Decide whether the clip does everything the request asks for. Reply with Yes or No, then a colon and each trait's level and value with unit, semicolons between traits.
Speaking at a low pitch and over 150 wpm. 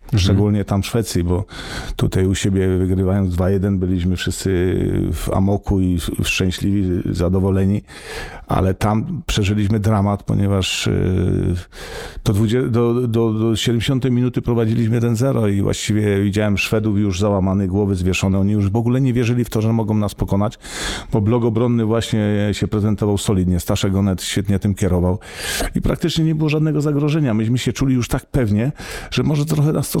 Yes: low, 105 Hz; fast, 160 wpm